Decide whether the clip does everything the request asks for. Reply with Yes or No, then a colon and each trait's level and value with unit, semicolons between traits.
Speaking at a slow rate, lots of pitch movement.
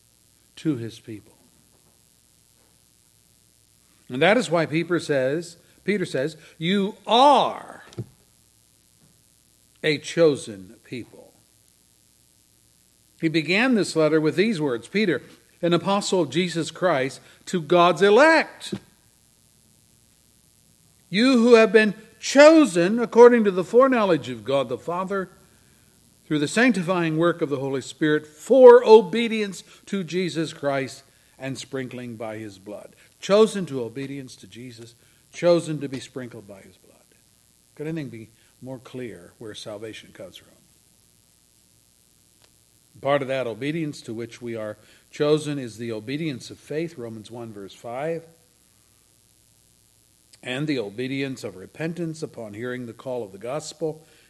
Yes: slow, 125 wpm; wide, 6.9 semitones